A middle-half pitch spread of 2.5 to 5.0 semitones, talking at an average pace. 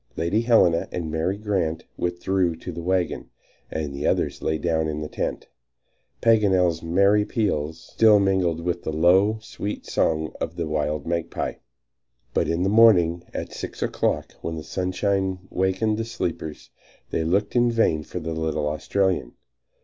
Yes: average, 3.7 semitones; average, 155 wpm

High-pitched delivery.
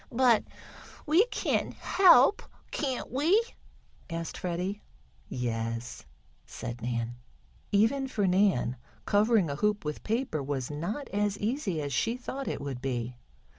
Yes: high, 195 Hz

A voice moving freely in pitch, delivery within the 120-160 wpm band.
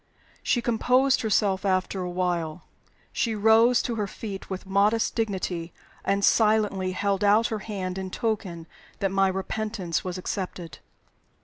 No: average, 2.9 semitones; average, 140 wpm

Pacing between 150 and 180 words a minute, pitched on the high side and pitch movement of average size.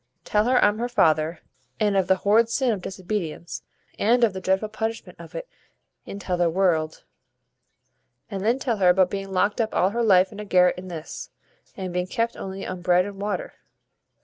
No: average, 195 wpm; high, 195 Hz; average, 3.3 semitones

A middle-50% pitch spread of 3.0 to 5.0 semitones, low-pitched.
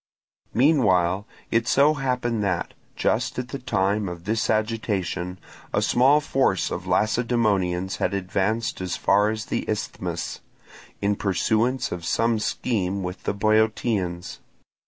Yes: average, 3.8 semitones; low, 110 Hz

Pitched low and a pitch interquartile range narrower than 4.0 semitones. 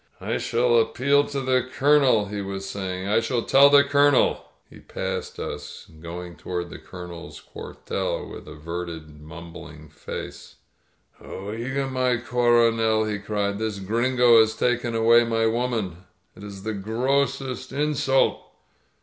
No: low, 115 Hz; average, 4.8 semitones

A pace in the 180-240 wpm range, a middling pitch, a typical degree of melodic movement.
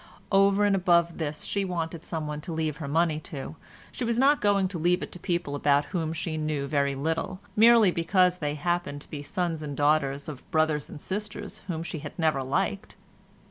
Yes: average, 200 wpm; medium, 165 Hz; average, 3.7 semitones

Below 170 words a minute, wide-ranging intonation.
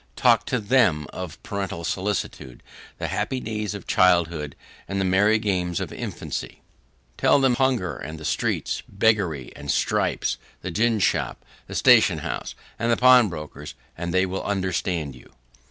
No: average, 155 wpm; average, 4.5 semitones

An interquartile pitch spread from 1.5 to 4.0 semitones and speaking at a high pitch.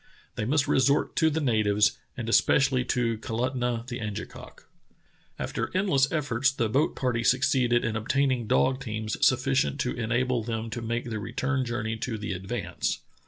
No: average, 3.0 semitones; low, 120 Hz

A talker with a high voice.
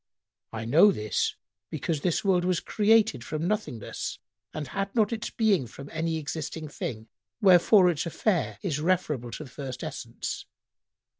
No: medium, 165 Hz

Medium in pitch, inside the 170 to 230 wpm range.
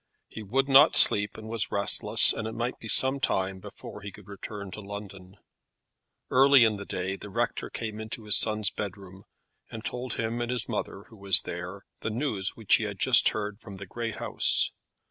No: low, 105 Hz; average, 200 wpm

